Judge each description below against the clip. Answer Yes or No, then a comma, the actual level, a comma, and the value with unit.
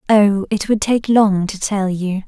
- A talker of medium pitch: No, high, 200 Hz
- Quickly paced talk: Yes, fast, 210 wpm